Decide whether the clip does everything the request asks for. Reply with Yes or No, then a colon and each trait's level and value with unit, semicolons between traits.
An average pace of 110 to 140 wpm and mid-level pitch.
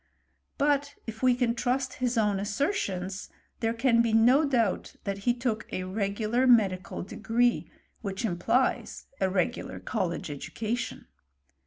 No: slow, 135 wpm; high, 225 Hz